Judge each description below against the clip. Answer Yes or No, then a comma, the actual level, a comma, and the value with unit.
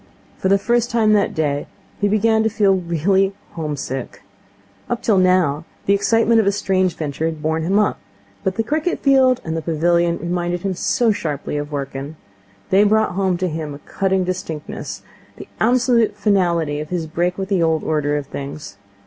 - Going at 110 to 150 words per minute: No, average, 190 wpm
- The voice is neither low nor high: Yes, medium, 180 Hz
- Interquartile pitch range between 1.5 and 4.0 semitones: No, average, 4.7 semitones